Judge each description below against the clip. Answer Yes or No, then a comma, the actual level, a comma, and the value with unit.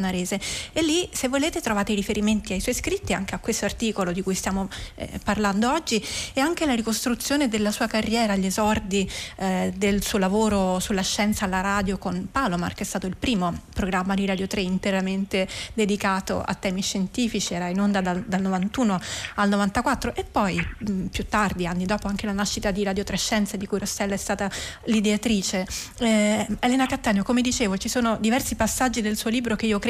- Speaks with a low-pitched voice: No, high, 205 Hz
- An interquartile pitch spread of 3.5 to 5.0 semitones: No, average, 2.8 semitones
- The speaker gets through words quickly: Yes, fast, 195 wpm